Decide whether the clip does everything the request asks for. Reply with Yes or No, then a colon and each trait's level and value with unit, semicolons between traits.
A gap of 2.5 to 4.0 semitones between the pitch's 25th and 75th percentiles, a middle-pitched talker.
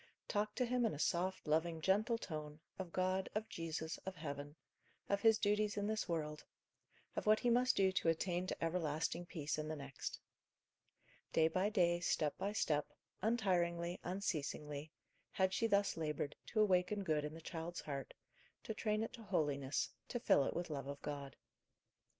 No: average, 5.0 semitones; medium, 175 Hz